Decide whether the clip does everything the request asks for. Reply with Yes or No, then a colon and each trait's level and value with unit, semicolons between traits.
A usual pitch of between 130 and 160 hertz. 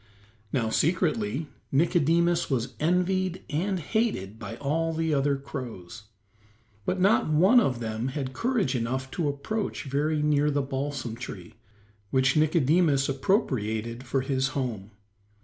Yes: medium, 140 Hz